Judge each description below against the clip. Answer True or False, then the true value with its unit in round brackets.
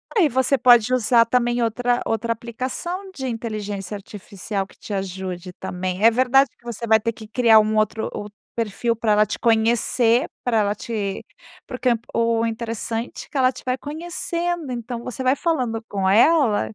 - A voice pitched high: True (230 Hz)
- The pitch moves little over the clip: False (3.0 semitones)